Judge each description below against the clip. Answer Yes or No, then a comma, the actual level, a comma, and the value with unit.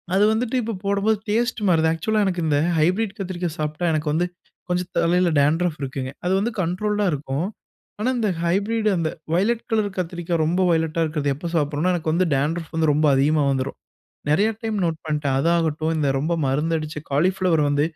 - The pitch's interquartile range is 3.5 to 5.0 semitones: Yes, average, 4.1 semitones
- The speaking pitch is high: No, medium, 170 Hz